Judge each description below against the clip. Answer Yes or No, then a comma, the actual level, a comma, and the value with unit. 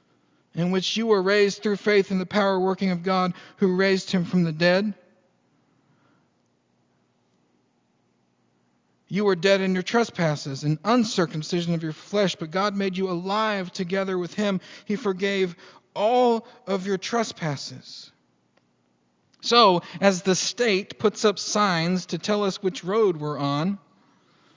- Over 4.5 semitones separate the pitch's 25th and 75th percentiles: No, average, 3.6 semitones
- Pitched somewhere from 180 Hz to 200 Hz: Yes, high, 190 Hz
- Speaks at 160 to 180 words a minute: No, average, 140 wpm